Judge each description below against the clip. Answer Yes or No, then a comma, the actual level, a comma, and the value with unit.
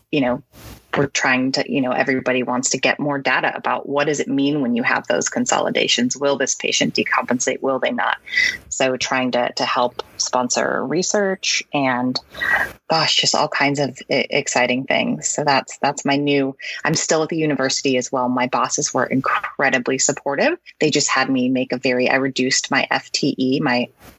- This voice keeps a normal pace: Yes, average, 185 wpm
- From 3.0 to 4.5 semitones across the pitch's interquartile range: No, narrow, 2.4 semitones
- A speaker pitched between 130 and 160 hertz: Yes, low, 135 Hz